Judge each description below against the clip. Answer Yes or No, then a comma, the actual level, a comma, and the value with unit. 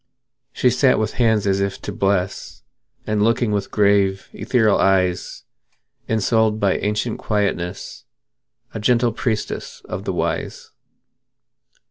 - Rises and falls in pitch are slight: Yes, narrow, 2.3 semitones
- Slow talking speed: Yes, slow, 120 wpm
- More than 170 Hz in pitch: No, low, 105 Hz